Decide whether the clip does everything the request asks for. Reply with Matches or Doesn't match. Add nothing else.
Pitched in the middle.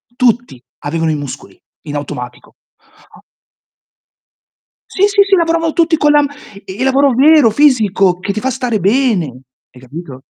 Doesn't match